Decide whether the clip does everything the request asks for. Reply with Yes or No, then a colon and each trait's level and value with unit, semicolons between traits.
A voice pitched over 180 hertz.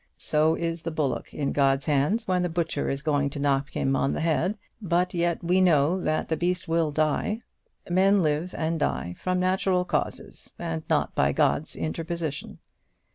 No: medium, 165 Hz